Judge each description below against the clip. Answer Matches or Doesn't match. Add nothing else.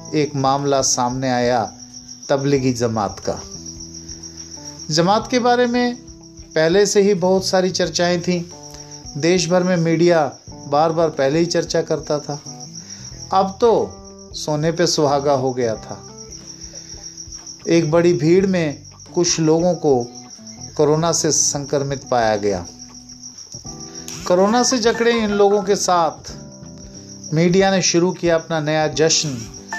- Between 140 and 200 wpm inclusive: Doesn't match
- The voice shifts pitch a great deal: Matches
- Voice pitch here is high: Doesn't match